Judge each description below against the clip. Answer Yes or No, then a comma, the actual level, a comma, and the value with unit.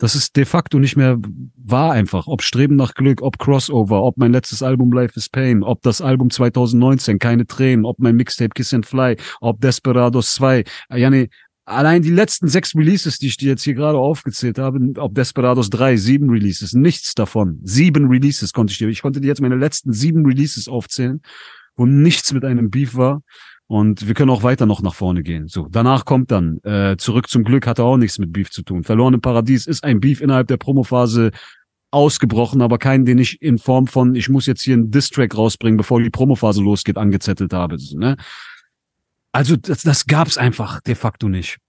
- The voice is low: Yes, low, 125 Hz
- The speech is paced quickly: Yes, fast, 205 wpm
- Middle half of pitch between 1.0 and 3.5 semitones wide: Yes, average, 3.1 semitones